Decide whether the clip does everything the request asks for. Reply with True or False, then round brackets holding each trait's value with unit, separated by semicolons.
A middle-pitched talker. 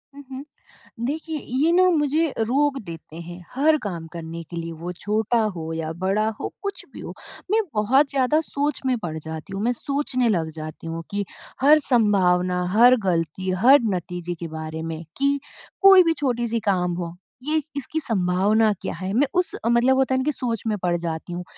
False (215 Hz)